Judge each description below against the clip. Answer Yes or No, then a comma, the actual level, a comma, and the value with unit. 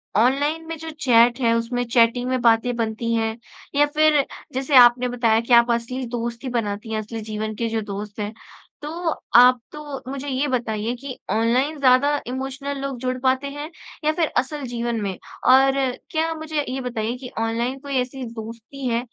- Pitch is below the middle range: No, very high, 250 Hz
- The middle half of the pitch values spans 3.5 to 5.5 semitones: No, average, 3.1 semitones